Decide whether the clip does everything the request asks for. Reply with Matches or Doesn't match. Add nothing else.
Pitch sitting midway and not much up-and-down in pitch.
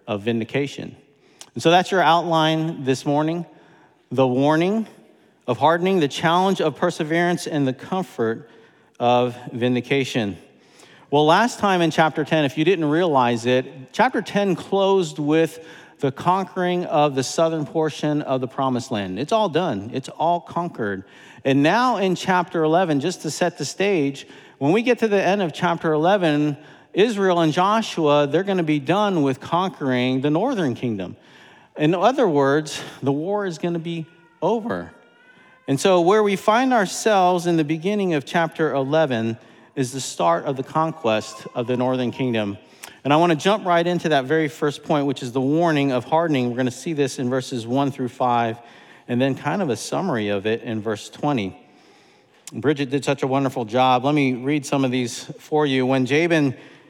Doesn't match